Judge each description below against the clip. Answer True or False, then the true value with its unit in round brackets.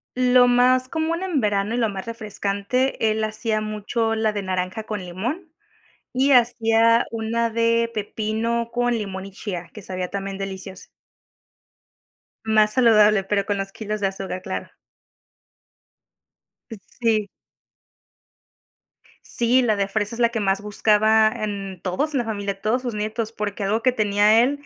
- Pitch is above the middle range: True (215 Hz)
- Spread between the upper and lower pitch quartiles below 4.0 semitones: True (2.6 semitones)